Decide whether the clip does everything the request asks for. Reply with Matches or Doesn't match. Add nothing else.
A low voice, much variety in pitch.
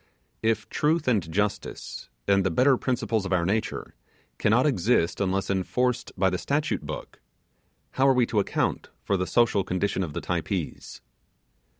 Doesn't match